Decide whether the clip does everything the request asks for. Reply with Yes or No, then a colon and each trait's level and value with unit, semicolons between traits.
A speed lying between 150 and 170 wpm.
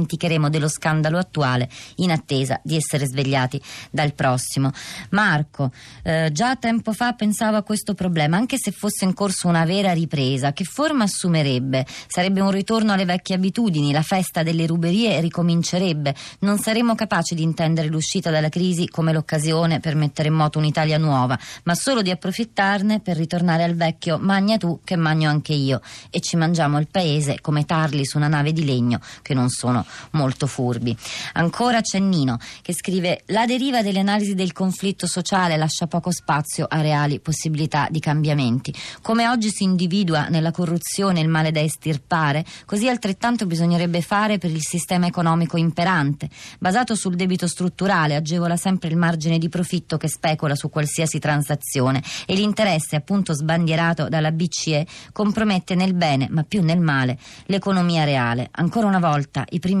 Yes: average, 165 wpm